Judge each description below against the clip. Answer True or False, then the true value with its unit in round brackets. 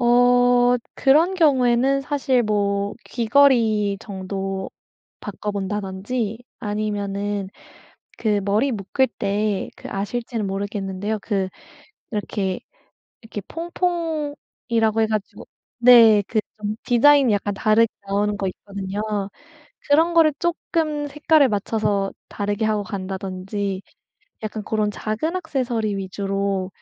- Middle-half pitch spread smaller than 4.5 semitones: True (3.8 semitones)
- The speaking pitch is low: False (215 Hz)